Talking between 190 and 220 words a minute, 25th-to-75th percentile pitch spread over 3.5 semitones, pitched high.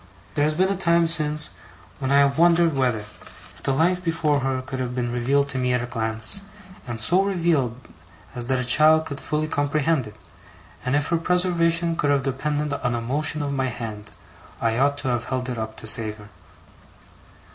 No: average, 200 wpm; average, 4.3 semitones; medium, 140 Hz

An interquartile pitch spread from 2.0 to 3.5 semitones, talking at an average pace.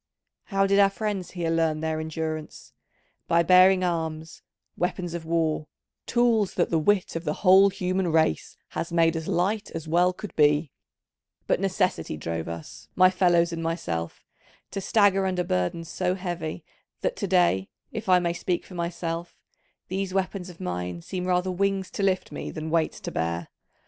Yes: average, 2.9 semitones; average, 170 wpm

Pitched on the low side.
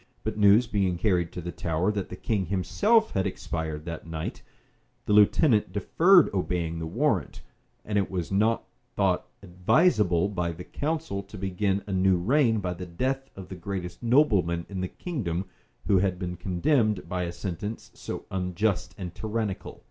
Yes: very low, 95 Hz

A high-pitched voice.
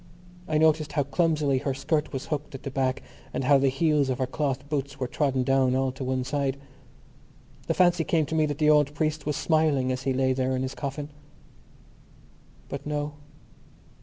No: medium, 140 Hz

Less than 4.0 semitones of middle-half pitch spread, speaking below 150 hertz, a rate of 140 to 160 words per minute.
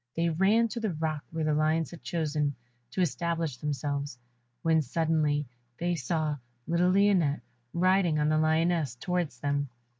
No: narrow, 2.6 semitones; medium, 160 Hz; average, 150 wpm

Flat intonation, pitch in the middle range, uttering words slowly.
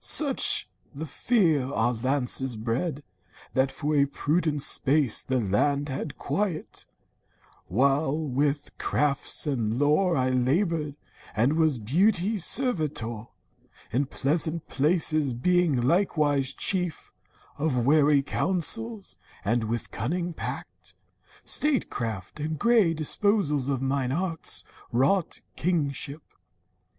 No: average, 4.3 semitones; medium, 145 Hz; slow, 105 wpm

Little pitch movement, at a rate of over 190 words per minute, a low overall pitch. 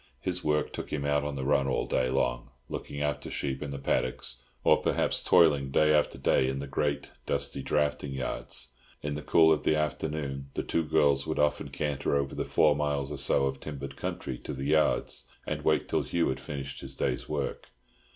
Yes: narrow, 1.7 semitones; fast, 205 wpm; very low, 70 Hz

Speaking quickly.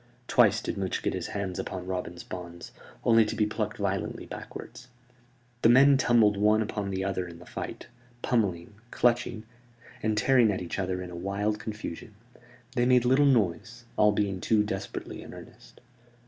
No: average, 170 wpm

